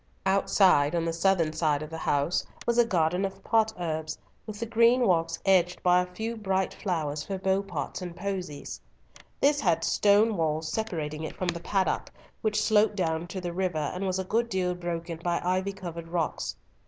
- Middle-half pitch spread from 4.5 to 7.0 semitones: No, average, 3.2 semitones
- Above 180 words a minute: Yes, average, 190 wpm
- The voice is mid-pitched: Yes, medium, 180 Hz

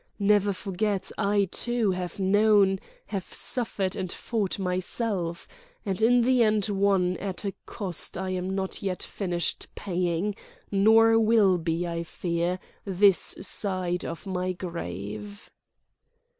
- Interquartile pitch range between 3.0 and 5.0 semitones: No, narrow, 2.4 semitones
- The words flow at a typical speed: No, slow, 120 wpm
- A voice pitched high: Yes, high, 195 Hz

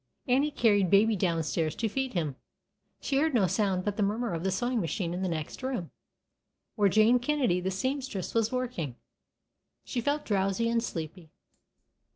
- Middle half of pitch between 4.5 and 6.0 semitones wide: Yes, wide, 5.4 semitones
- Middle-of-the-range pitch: No, high, 205 Hz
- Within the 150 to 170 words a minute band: No, average, 180 wpm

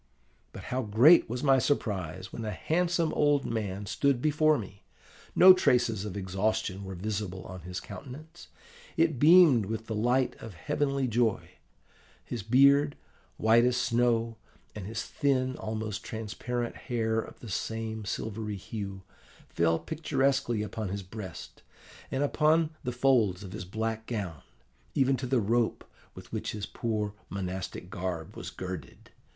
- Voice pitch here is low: Yes, low, 110 Hz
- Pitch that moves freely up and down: No, average, 4.8 semitones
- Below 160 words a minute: Yes, average, 150 wpm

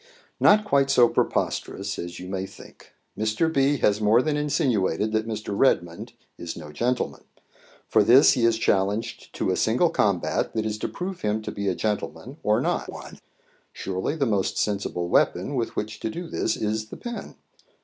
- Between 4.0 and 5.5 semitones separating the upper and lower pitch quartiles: Yes, average, 5.1 semitones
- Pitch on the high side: No, low, 110 Hz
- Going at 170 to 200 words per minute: Yes, average, 180 wpm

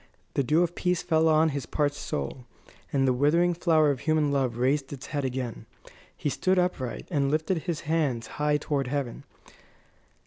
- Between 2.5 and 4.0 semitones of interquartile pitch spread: Yes, average, 3.2 semitones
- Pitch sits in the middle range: Yes, medium, 145 Hz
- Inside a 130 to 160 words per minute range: No, average, 175 wpm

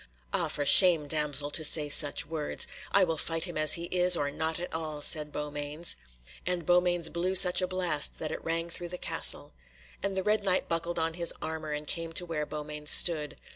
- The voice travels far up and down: No, average, 2.8 semitones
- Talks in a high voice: No, medium, 165 Hz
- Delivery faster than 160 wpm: Yes, average, 200 wpm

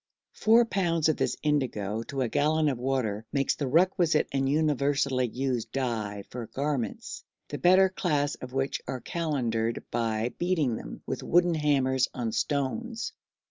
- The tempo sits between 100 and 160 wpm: Yes, average, 150 wpm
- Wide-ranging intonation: No, average, 4.2 semitones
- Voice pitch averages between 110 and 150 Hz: Yes, low, 135 Hz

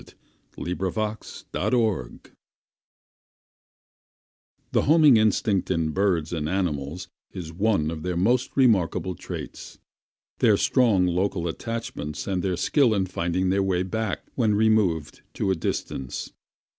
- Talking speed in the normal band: No, slow, 130 wpm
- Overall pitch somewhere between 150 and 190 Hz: No, very low, 95 Hz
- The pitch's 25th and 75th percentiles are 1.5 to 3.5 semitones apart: No, average, 4.3 semitones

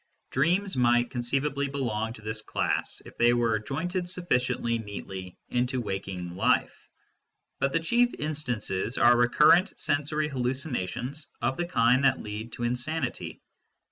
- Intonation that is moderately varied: Yes, average, 4.5 semitones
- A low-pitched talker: Yes, low, 125 Hz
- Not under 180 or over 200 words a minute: No, slow, 135 wpm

